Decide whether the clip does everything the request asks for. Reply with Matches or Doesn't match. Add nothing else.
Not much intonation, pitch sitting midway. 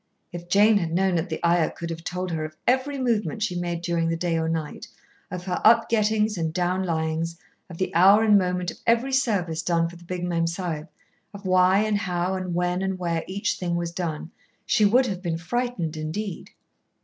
Doesn't match